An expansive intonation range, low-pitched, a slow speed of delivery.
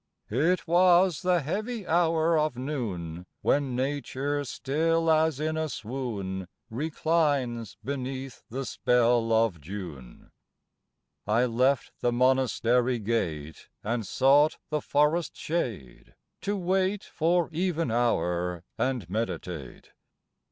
Yes: wide, 5.9 semitones; low, 130 Hz; slow, 110 wpm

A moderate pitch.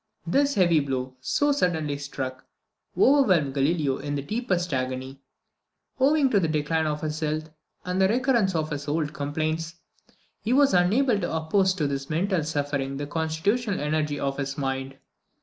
Yes: medium, 155 Hz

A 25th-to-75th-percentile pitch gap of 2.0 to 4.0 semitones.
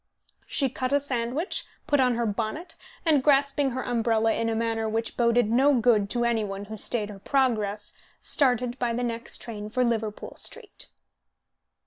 Yes: average, 2.8 semitones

